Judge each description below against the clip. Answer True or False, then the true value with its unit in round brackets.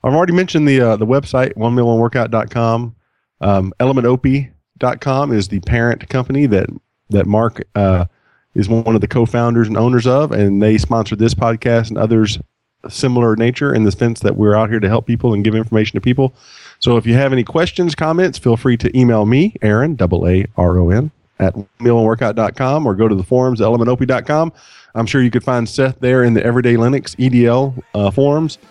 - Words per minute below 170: False (185 wpm)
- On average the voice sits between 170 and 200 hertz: False (120 Hz)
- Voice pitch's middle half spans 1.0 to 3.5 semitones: True (2.9 semitones)